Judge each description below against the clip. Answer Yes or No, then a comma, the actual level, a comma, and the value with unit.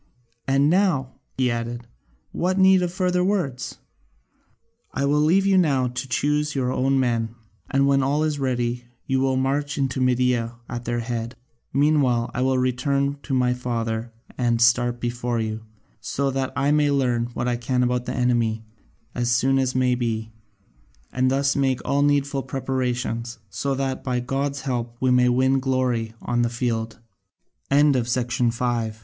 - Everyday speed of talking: Yes, average, 150 wpm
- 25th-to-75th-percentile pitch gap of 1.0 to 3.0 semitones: Yes, narrow, 2.5 semitones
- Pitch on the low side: Yes, low, 130 Hz